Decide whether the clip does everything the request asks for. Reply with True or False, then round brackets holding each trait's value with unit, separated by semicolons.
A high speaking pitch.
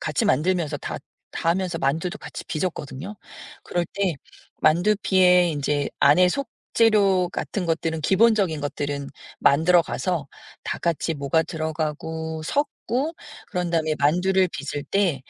False (170 Hz)